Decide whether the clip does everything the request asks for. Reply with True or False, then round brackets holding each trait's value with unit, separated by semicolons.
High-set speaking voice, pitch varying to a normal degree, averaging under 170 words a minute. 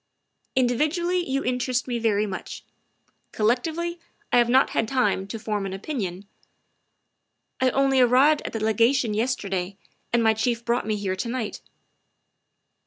True (235 Hz; 3.6 semitones; 155 wpm)